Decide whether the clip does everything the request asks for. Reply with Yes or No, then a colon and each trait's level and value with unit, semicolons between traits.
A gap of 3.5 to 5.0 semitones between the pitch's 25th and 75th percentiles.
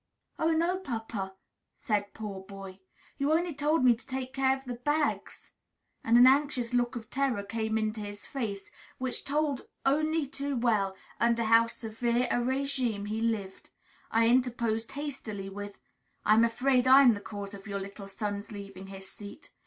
Yes: average, 4.7 semitones